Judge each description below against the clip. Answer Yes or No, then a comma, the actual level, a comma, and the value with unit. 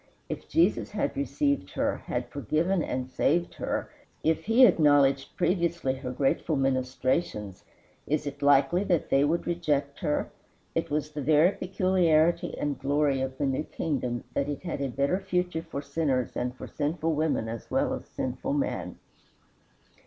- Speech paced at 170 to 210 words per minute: No, average, 160 wpm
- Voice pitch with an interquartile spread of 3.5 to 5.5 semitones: Yes, average, 3.9 semitones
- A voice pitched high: No, medium, 150 Hz